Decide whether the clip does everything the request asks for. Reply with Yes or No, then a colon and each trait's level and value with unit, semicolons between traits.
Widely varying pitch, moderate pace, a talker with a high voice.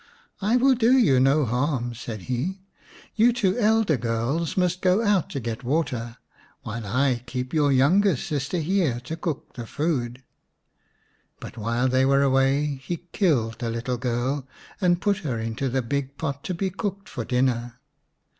No: wide, 6.6 semitones; average, 175 wpm; medium, 140 Hz